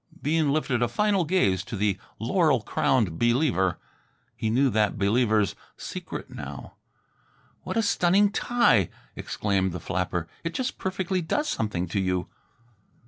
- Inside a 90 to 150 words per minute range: Yes, average, 140 wpm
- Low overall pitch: Yes, low, 120 Hz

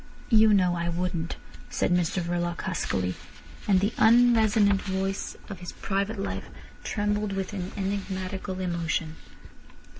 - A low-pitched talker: No, high, 190 Hz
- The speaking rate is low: Yes, slow, 125 wpm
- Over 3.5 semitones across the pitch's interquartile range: No, narrow, 2.6 semitones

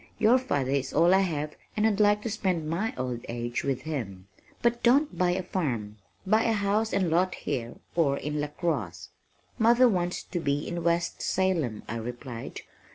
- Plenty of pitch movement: Yes, wide, 7.1 semitones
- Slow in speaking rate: No, average, 180 wpm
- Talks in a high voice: No, medium, 170 Hz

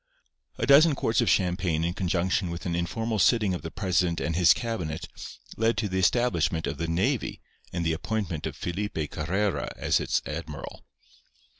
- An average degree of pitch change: Yes, average, 4.2 semitones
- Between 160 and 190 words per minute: Yes, average, 170 wpm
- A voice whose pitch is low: Yes, very low, 90 Hz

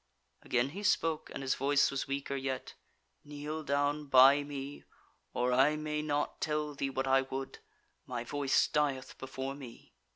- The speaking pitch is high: No, medium, 140 Hz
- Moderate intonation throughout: No, narrow, 1.8 semitones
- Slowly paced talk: No, average, 160 wpm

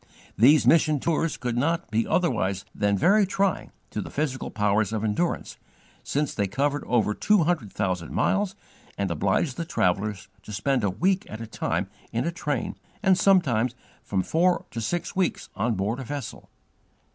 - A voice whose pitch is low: Yes, low, 125 Hz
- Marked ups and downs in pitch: Yes, wide, 8.2 semitones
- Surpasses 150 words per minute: Yes, average, 170 wpm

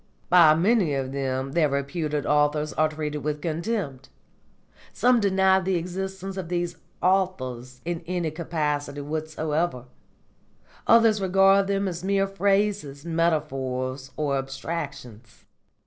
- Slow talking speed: Yes, slow, 115 wpm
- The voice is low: No, medium, 160 Hz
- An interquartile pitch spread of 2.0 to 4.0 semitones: No, average, 5.0 semitones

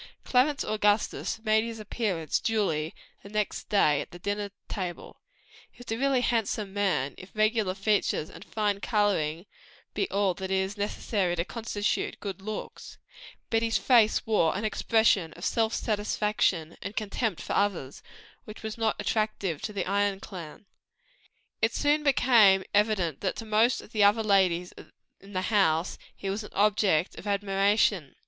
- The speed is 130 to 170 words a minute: Yes, average, 160 wpm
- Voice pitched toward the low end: No, high, 205 Hz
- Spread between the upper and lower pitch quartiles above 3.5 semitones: No, narrow, 2.5 semitones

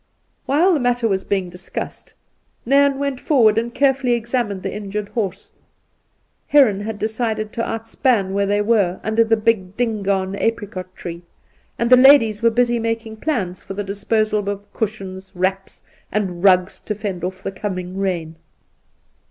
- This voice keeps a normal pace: Yes, average, 155 wpm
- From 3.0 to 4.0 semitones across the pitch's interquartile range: Yes, average, 3.3 semitones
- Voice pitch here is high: Yes, high, 210 Hz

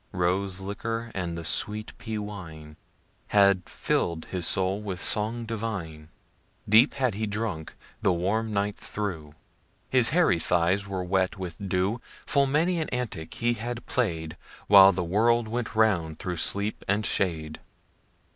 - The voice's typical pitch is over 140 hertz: No, low, 100 Hz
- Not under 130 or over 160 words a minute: Yes, average, 150 wpm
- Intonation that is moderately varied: Yes, average, 4.1 semitones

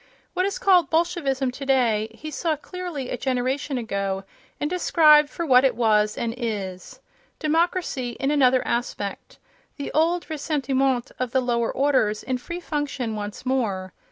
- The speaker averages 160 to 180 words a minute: No, average, 145 wpm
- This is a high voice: Yes, very high, 265 Hz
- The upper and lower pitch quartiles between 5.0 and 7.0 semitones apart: No, average, 4.6 semitones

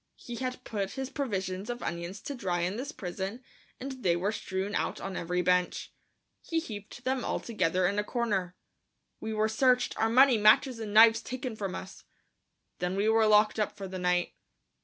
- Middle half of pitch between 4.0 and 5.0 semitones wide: Yes, average, 4.4 semitones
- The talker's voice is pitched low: No, high, 210 Hz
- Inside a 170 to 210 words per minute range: Yes, average, 190 wpm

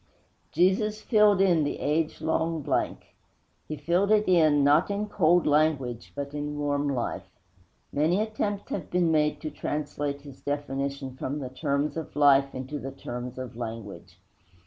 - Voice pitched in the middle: Yes, medium, 145 Hz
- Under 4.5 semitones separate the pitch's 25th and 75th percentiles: Yes, average, 3.5 semitones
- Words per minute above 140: Yes, average, 155 wpm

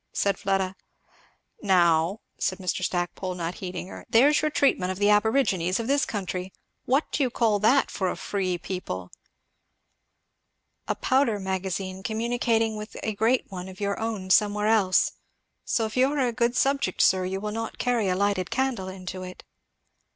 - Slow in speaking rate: No, average, 170 wpm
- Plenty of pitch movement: No, average, 3.5 semitones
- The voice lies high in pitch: Yes, high, 200 Hz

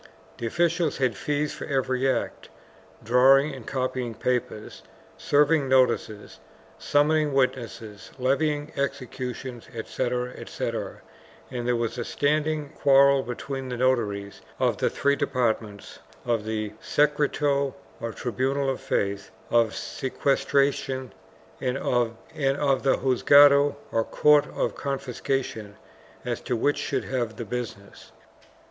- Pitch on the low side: Yes, low, 130 Hz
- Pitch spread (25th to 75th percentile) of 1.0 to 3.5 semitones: Yes, average, 3.0 semitones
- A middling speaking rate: No, slow, 125 wpm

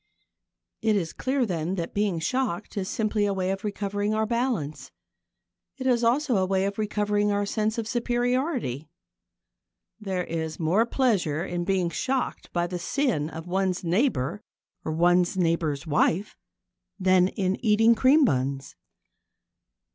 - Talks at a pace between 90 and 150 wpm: Yes, average, 145 wpm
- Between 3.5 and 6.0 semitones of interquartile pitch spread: Yes, average, 4.6 semitones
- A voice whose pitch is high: Yes, high, 195 Hz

